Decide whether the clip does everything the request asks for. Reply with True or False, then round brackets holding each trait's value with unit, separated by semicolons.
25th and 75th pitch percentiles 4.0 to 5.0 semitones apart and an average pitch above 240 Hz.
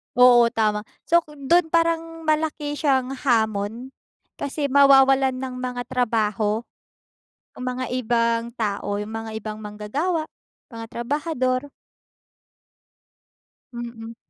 True (4.3 semitones; 250 Hz)